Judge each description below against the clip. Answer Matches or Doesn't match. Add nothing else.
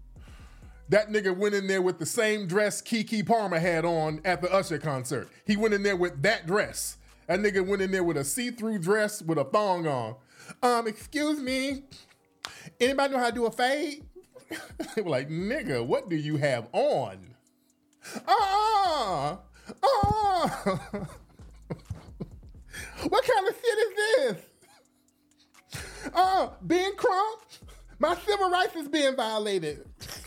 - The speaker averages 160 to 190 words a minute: Doesn't match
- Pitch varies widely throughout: Matches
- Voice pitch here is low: Doesn't match